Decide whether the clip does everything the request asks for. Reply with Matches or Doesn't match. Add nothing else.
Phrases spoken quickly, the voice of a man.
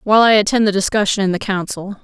Doesn't match